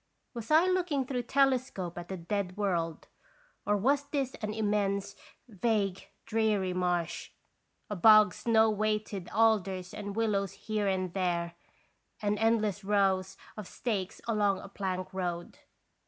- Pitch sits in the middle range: No, high, 205 Hz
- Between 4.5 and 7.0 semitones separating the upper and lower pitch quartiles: No, average, 3.0 semitones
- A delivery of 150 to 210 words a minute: No, slow, 135 wpm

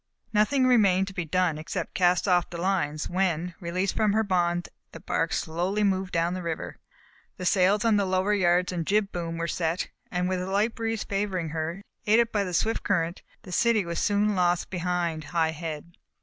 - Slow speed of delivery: No, average, 200 wpm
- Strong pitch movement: No, average, 2.9 semitones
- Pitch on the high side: No, medium, 180 Hz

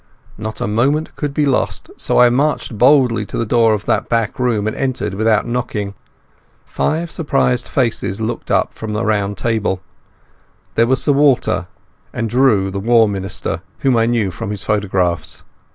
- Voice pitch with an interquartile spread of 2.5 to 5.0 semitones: Yes, average, 3.5 semitones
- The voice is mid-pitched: No, low, 115 Hz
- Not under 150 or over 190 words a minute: Yes, average, 170 wpm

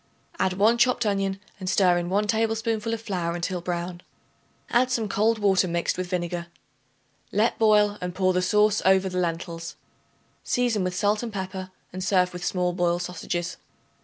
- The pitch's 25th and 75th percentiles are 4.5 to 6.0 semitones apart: No, average, 3.0 semitones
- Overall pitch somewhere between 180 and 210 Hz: Yes, high, 190 Hz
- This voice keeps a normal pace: Yes, average, 170 wpm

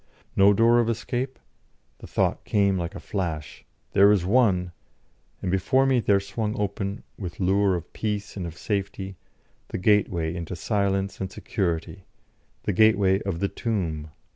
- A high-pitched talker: No, low, 100 Hz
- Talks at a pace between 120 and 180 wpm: Yes, average, 155 wpm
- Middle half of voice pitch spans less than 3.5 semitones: Yes, narrow, 2.5 semitones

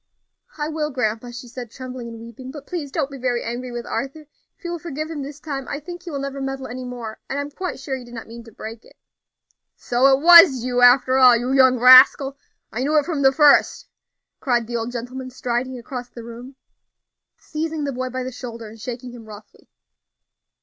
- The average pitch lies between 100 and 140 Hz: No, very high, 255 Hz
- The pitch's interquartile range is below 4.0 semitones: Yes, narrow, 2.6 semitones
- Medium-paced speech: No, fast, 220 wpm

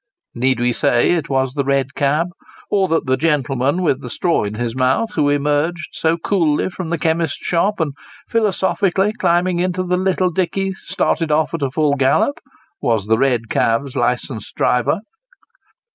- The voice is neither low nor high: Yes, medium, 150 Hz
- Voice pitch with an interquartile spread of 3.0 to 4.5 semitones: No, average, 5.1 semitones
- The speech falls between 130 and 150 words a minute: No, average, 165 wpm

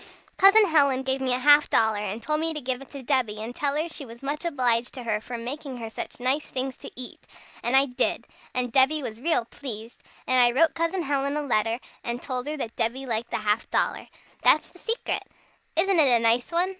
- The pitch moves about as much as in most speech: Yes, average, 4.0 semitones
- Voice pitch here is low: No, very high, 260 Hz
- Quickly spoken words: Yes, fast, 230 wpm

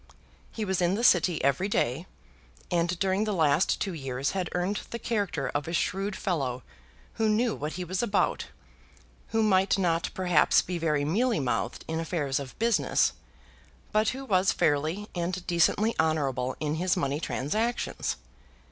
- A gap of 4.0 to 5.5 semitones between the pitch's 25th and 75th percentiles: Yes, average, 5.0 semitones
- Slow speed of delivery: No, average, 160 wpm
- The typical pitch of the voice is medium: Yes, medium, 180 Hz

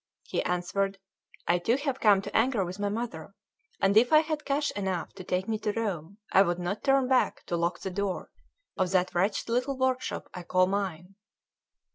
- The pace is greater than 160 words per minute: Yes, average, 195 wpm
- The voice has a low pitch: No, high, 200 Hz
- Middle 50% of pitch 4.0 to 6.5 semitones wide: Yes, average, 5.1 semitones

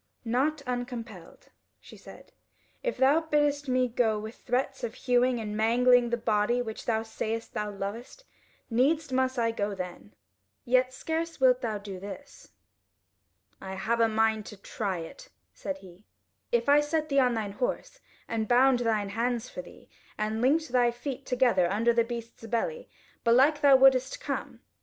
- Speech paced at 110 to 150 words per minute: No, average, 165 wpm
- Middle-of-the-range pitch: No, high, 240 Hz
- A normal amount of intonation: Yes, average, 3.4 semitones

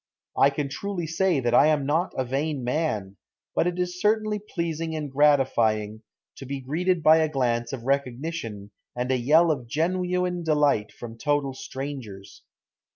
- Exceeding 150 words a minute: Yes, average, 160 wpm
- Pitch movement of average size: Yes, average, 4.9 semitones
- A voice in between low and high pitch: Yes, medium, 145 Hz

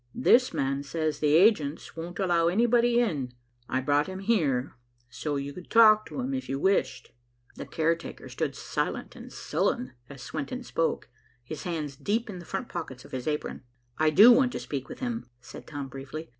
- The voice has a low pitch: No, medium, 165 Hz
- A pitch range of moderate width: No, wide, 7.3 semitones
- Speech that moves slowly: No, average, 185 wpm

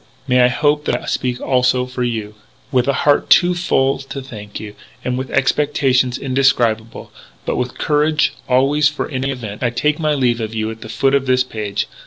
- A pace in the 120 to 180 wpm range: No, average, 200 wpm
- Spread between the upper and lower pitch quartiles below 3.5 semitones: Yes, narrow, 2.6 semitones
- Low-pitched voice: Yes, low, 130 Hz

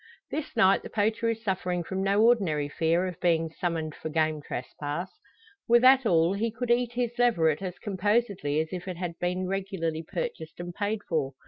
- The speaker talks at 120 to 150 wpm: No, average, 190 wpm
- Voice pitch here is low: No, medium, 185 Hz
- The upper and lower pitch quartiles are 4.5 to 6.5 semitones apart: Yes, average, 5.1 semitones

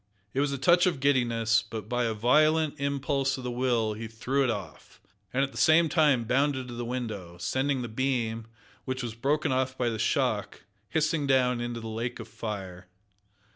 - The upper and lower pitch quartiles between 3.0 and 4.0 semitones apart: Yes, average, 3.5 semitones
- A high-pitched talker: No, low, 125 Hz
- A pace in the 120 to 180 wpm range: No, average, 195 wpm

